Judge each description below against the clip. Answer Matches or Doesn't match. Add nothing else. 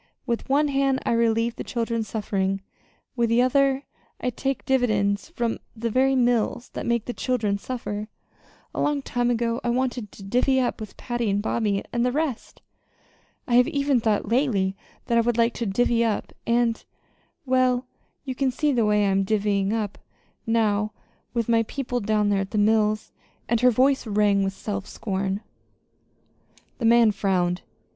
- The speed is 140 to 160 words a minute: Doesn't match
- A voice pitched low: Doesn't match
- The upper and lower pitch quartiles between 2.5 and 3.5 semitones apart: Matches